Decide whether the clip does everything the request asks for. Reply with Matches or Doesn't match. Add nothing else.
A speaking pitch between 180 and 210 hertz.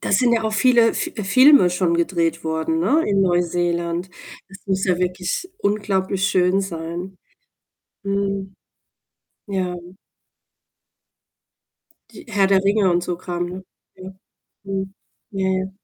Matches